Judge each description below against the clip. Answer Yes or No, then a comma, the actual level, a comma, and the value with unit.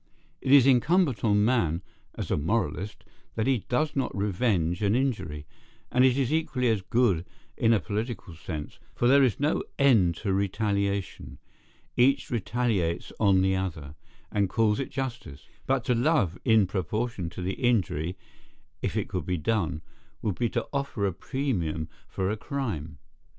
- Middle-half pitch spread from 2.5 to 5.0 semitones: No, wide, 5.5 semitones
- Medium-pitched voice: No, low, 105 Hz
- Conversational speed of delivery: Yes, average, 160 wpm